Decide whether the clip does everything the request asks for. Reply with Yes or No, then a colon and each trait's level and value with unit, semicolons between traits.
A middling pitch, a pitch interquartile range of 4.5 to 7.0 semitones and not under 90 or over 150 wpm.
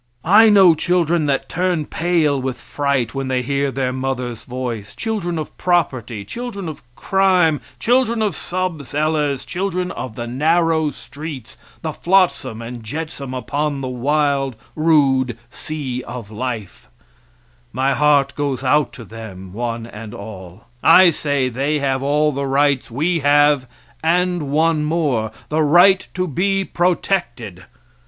Yes: medium, 145 Hz; average, 4.8 semitones; average, 140 wpm